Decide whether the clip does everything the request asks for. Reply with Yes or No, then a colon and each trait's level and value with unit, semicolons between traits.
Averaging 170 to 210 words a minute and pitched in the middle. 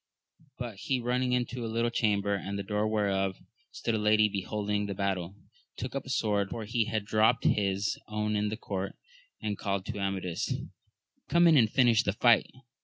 No: average, 185 wpm; low, 105 Hz